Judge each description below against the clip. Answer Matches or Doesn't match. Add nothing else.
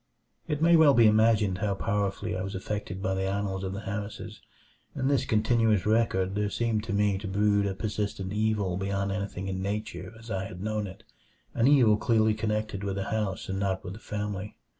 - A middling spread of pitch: Doesn't match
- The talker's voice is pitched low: Matches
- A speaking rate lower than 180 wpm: Doesn't match